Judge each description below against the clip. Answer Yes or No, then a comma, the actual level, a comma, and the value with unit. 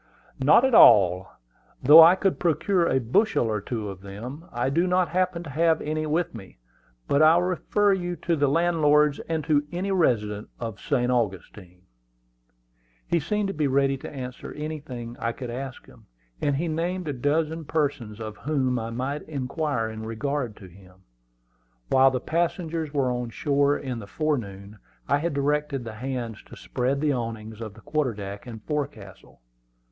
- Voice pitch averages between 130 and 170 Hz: Yes, medium, 140 Hz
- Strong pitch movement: Yes, wide, 5.7 semitones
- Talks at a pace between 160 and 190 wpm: Yes, average, 175 wpm